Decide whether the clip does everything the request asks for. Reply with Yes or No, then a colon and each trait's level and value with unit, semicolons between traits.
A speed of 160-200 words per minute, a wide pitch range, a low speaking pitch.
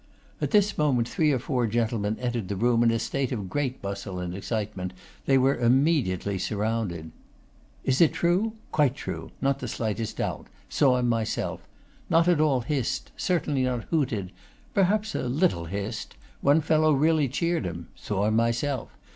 Yes: average, 165 wpm; wide, 5.8 semitones; low, 125 Hz